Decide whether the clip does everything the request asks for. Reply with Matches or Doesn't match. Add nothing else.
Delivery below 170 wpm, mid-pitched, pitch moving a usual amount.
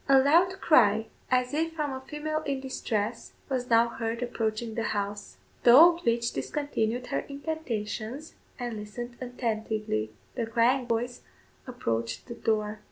Doesn't match